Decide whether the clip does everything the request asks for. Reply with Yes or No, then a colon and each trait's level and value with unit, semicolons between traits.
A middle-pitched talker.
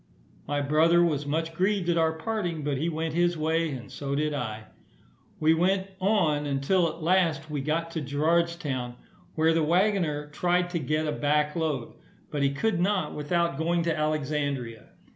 Yes: medium, 160 Hz